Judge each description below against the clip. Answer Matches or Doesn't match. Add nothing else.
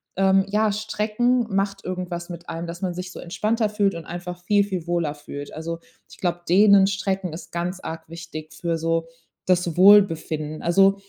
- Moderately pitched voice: Matches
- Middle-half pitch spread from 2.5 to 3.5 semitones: Matches